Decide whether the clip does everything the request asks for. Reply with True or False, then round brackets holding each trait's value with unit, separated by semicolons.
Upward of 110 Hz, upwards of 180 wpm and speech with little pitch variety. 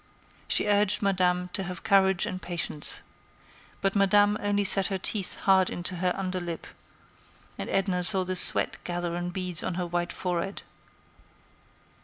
False (185 Hz; 155 wpm; 1.7 semitones)